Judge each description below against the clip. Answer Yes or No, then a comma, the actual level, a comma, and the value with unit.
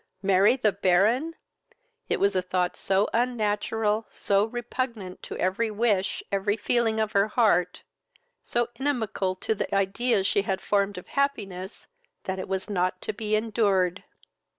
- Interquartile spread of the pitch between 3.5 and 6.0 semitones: No, average, 2.9 semitones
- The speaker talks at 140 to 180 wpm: Yes, average, 150 wpm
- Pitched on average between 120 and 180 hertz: No, high, 205 Hz